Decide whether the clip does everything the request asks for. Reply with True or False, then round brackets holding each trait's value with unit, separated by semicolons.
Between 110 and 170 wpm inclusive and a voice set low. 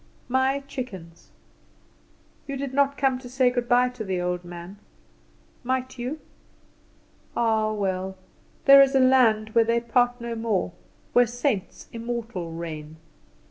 False (140 wpm; 235 Hz)